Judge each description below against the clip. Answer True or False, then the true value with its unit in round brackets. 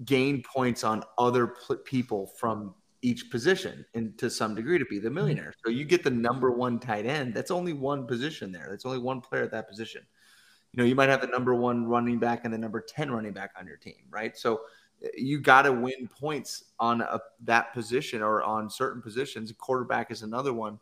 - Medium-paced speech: False (215 wpm)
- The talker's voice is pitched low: True (120 Hz)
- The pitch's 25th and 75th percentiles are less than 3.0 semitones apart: True (2.5 semitones)